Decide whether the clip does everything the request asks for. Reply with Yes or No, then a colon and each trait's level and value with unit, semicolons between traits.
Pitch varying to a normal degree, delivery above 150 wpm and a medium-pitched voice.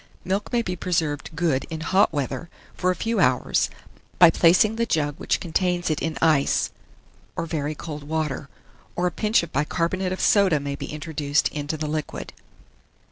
Yes: average, 3.6 semitones; average, 175 wpm; medium, 160 Hz